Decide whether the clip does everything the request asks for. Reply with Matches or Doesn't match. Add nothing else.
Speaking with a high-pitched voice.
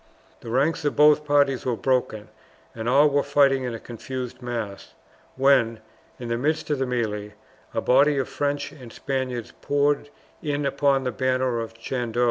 Doesn't match